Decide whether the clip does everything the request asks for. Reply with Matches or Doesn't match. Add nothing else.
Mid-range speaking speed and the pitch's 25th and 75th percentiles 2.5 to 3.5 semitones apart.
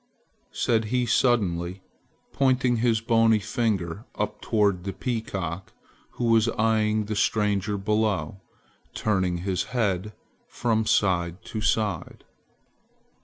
Doesn't match